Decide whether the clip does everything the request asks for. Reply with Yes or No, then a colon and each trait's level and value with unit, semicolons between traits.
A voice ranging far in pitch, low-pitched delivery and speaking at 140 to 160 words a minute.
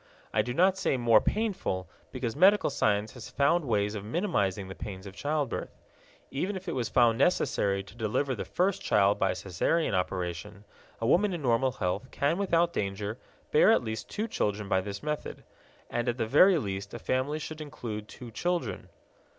No: wide, 7.5 semitones; low, 120 Hz; average, 185 wpm